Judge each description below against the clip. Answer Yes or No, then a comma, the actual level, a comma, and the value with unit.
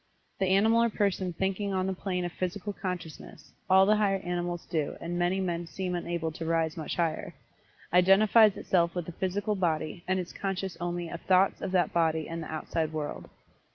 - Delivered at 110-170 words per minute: No, average, 190 wpm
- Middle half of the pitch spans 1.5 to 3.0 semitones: Yes, narrow, 2.4 semitones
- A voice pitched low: No, medium, 180 Hz